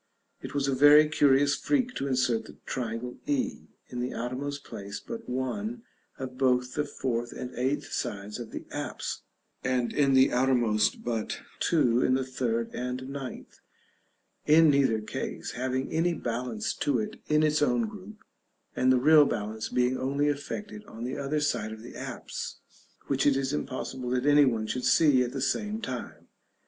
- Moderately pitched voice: No, low, 130 Hz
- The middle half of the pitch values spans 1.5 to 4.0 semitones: Yes, average, 3.1 semitones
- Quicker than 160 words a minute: Yes, average, 175 wpm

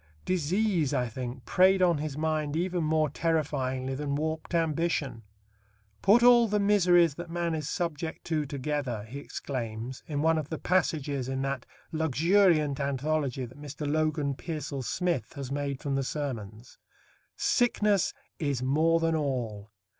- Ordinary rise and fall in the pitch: Yes, average, 3.7 semitones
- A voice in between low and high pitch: Yes, medium, 150 Hz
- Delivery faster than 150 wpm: No, average, 145 wpm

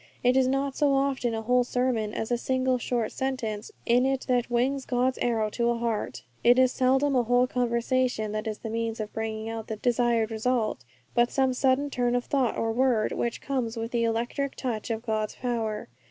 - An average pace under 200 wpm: No, fast, 205 wpm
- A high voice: Yes, high, 240 Hz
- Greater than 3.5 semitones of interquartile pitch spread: No, narrow, 2.4 semitones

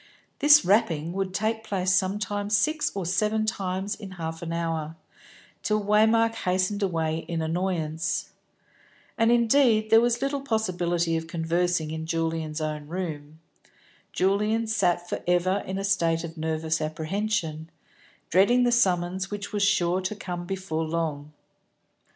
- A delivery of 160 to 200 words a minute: No, average, 140 wpm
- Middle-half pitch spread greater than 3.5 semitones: Yes, average, 4.3 semitones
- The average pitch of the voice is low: No, medium, 185 Hz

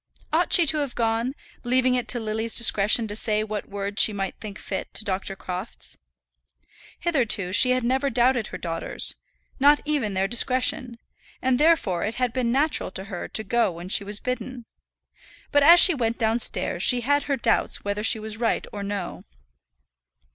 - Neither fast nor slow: Yes, average, 180 wpm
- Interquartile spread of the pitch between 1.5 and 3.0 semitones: No, average, 4.0 semitones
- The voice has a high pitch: Yes, high, 230 Hz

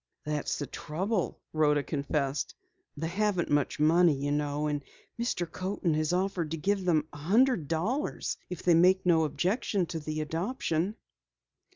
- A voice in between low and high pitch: Yes, medium, 165 Hz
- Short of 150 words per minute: No, average, 155 wpm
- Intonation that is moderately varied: Yes, average, 3.8 semitones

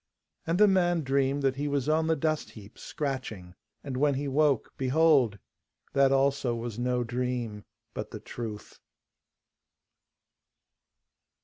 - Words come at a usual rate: No, slow, 130 wpm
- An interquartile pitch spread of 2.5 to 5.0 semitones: Yes, average, 3.4 semitones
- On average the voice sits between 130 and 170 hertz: Yes, low, 135 Hz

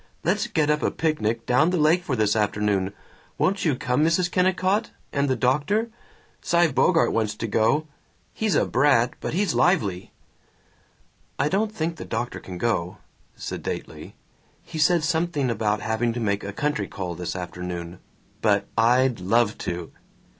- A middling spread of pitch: No, wide, 7.9 semitones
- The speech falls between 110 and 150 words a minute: No, average, 160 wpm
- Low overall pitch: Yes, low, 130 Hz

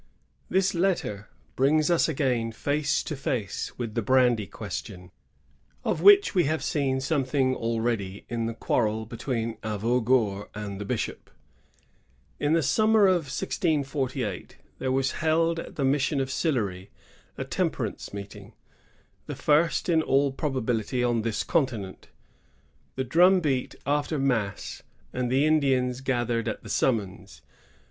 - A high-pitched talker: No, low, 130 Hz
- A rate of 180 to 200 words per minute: No, average, 140 wpm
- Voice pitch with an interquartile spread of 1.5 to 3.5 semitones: No, average, 4.8 semitones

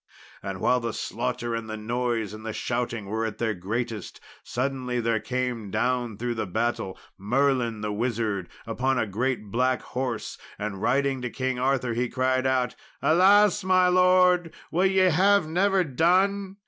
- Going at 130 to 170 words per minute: Yes, average, 160 wpm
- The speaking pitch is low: Yes, low, 125 Hz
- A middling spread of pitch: Yes, average, 3.9 semitones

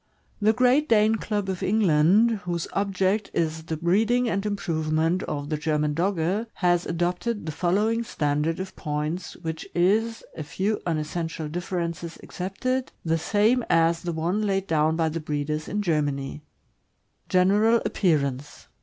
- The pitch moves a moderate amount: Yes, average, 4.5 semitones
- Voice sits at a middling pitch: Yes, medium, 175 Hz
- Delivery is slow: No, average, 145 wpm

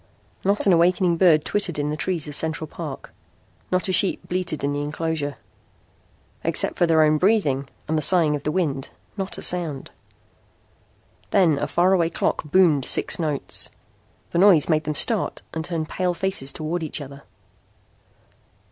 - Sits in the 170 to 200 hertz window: No, medium, 160 Hz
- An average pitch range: Yes, average, 3.4 semitones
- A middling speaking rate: Yes, average, 165 wpm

